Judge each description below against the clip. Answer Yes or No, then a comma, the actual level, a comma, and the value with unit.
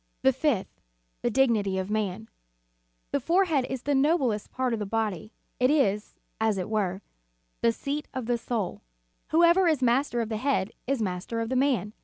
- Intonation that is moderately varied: Yes, average, 4.5 semitones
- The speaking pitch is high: Yes, high, 235 Hz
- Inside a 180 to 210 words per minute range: Yes, average, 190 wpm